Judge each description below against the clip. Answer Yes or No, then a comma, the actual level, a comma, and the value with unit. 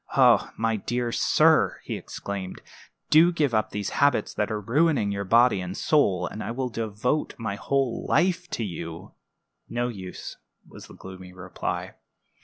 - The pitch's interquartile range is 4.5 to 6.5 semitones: Yes, average, 5.1 semitones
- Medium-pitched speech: No, low, 115 Hz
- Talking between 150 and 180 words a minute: Yes, average, 155 wpm